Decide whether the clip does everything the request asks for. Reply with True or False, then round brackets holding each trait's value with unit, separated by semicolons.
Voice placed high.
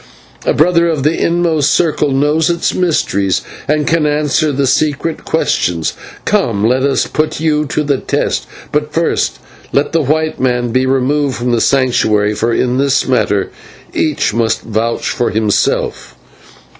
False (140 Hz)